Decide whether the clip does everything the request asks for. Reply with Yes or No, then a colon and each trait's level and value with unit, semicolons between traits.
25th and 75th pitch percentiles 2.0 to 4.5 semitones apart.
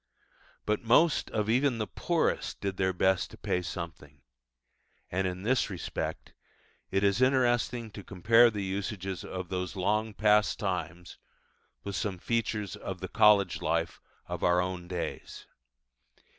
Yes: average, 3.0 semitones